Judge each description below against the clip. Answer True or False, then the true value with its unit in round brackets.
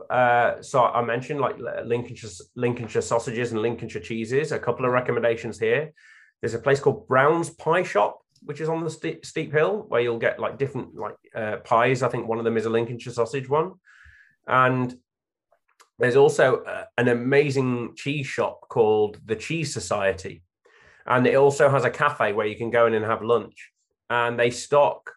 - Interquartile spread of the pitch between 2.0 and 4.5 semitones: True (3.4 semitones)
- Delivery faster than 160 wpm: True (180 wpm)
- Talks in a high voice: False (120 Hz)